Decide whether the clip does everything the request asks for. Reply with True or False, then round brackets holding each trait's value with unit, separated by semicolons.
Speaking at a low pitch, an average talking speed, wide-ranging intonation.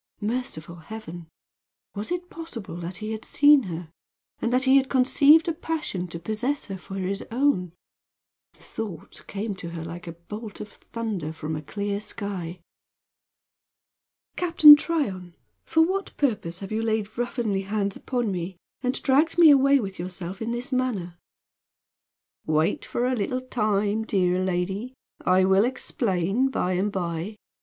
False (210 Hz; 155 wpm; 5.9 semitones)